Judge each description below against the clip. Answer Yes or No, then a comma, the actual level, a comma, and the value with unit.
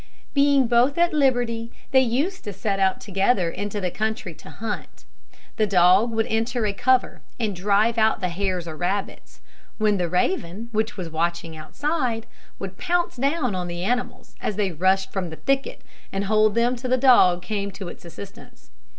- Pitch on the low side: No, high, 215 Hz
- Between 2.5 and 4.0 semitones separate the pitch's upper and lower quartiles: No, average, 4.6 semitones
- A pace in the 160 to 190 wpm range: Yes, average, 180 wpm